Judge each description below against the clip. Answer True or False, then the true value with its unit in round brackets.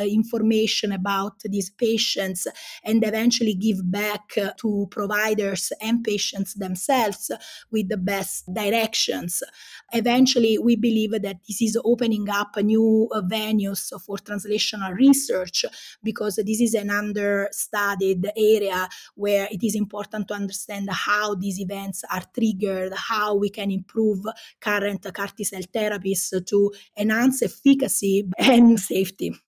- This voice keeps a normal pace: False (120 wpm)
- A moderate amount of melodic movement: False (1.8 semitones)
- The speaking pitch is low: False (210 Hz)